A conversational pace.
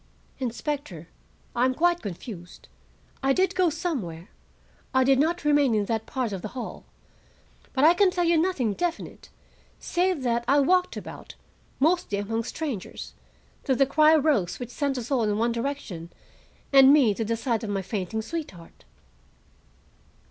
Yes: average, 160 wpm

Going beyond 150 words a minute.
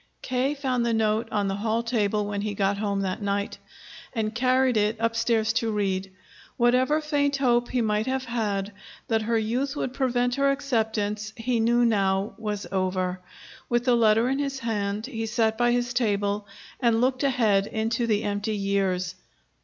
Yes: average, 175 wpm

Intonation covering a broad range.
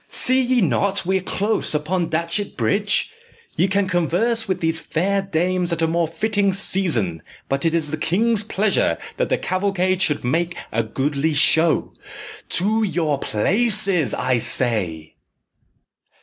No: average, 4.2 semitones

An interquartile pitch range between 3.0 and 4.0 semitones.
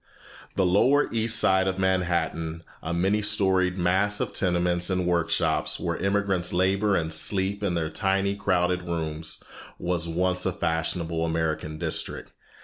No: narrow, 2.5 semitones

